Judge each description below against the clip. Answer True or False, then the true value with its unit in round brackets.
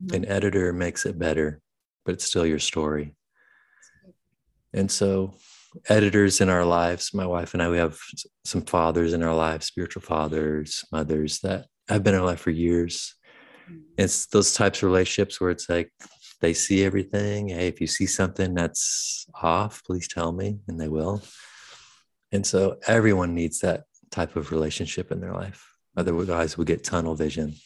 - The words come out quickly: False (170 wpm)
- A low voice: True (85 Hz)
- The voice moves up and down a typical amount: True (3.0 semitones)